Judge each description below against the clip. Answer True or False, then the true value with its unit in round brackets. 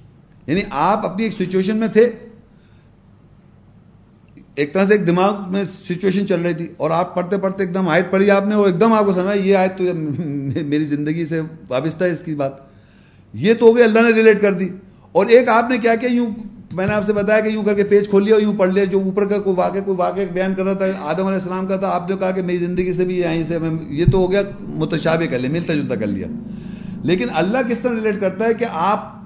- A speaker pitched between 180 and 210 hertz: True (190 Hz)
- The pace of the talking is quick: True (250 wpm)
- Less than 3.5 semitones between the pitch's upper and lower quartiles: True (3.1 semitones)